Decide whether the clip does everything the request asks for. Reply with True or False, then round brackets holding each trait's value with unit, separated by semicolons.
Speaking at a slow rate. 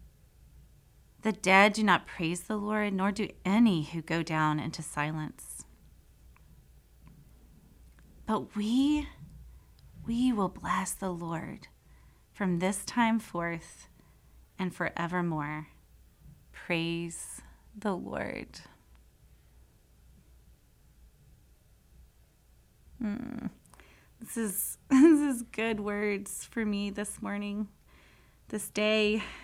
True (90 wpm)